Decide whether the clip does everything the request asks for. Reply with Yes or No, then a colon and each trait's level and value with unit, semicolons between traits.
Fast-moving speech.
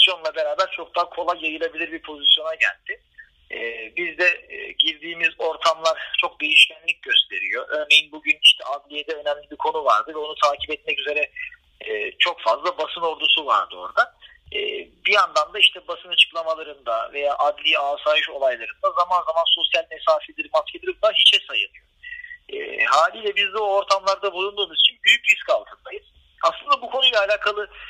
Yes: fast, 145 wpm